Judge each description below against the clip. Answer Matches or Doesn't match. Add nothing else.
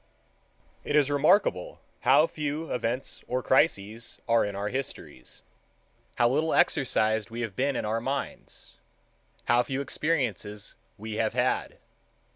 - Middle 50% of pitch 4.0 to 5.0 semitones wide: Matches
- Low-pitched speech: Matches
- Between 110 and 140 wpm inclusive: Matches